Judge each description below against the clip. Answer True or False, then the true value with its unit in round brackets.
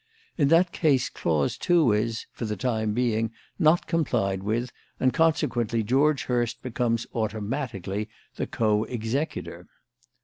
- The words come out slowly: True (130 wpm)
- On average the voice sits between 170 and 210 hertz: False (120 Hz)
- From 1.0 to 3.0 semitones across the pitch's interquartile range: False (4.1 semitones)